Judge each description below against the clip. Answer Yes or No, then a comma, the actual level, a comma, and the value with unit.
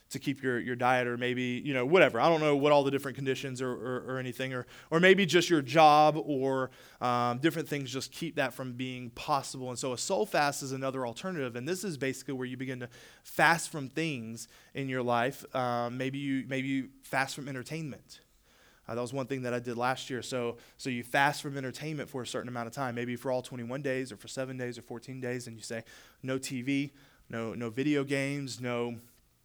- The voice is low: Yes, low, 130 Hz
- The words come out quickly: Yes, fast, 230 wpm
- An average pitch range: No, narrow, 2.2 semitones